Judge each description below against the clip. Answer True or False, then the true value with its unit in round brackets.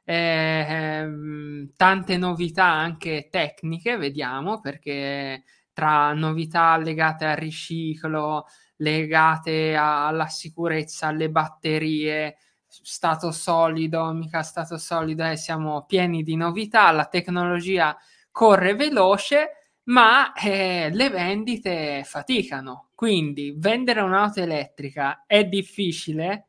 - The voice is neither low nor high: True (160 Hz)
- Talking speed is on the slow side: True (100 wpm)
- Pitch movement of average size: True (3.4 semitones)